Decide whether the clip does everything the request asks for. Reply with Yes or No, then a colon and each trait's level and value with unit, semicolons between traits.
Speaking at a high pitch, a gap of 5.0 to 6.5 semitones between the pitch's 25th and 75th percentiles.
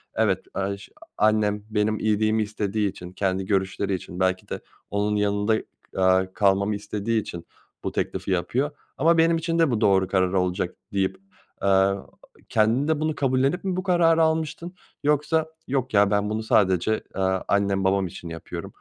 No: low, 105 Hz; average, 5.3 semitones